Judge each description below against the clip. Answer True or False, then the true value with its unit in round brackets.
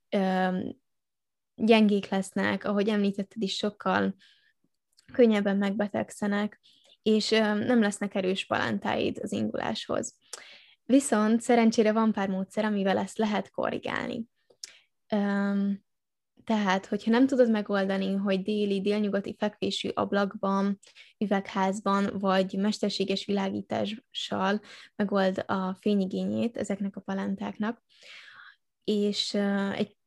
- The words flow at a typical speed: False (90 wpm)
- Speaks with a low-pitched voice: False (205 Hz)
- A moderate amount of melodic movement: False (1.8 semitones)